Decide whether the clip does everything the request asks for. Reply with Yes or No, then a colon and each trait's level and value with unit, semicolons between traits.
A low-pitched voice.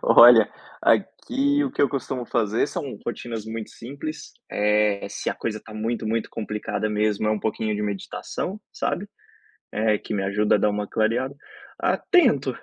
Yes: low, 110 Hz